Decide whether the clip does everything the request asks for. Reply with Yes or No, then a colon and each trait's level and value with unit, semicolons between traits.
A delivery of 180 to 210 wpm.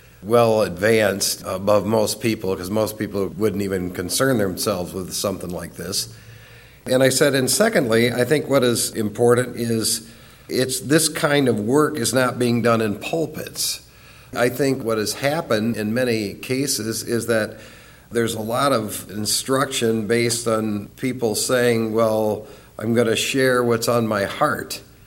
No: average, 160 wpm